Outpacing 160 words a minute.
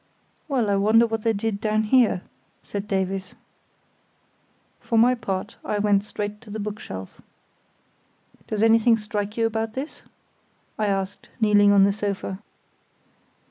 No: average, 140 wpm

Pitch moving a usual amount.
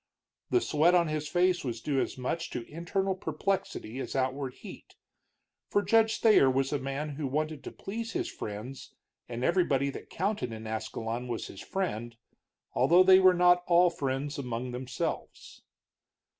No: wide, 5.9 semitones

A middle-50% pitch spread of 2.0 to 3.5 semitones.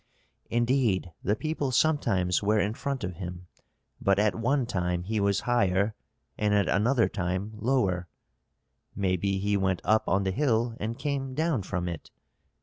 No: average, 4.6 semitones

